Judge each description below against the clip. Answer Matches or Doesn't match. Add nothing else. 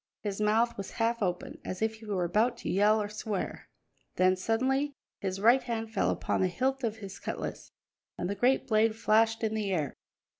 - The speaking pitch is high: Matches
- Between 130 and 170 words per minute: Doesn't match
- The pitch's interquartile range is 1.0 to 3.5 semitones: Matches